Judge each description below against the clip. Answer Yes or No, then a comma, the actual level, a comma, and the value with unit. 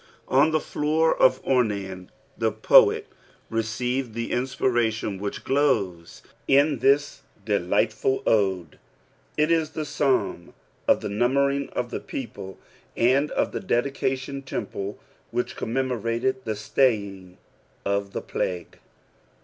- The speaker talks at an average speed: No, slow, 115 wpm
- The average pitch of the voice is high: No, low, 120 Hz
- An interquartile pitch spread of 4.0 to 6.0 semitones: Yes, average, 4.8 semitones